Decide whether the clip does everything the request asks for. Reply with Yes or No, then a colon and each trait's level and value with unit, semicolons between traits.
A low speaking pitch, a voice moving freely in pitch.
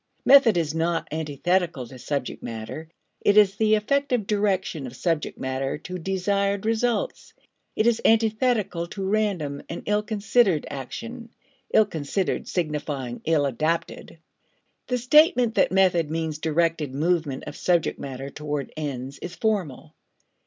No: medium, 170 Hz; wide, 6.1 semitones